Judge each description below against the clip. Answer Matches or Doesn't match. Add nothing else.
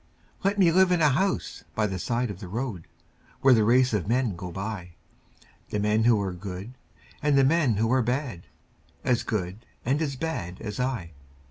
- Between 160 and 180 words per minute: Doesn't match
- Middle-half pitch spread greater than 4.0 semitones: Matches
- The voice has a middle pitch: Doesn't match